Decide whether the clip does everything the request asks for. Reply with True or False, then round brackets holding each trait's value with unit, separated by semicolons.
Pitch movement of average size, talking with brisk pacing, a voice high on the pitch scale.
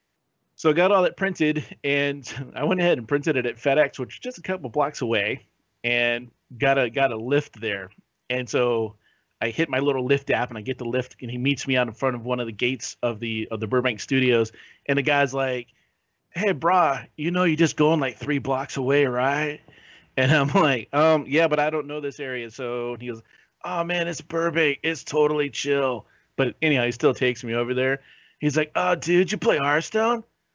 False (3.9 semitones; 220 wpm; 140 Hz)